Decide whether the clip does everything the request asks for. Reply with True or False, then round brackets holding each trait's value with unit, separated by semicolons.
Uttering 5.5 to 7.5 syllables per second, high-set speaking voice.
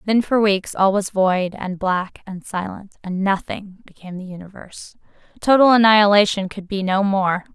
False (4.9 syllables/s; 195 Hz)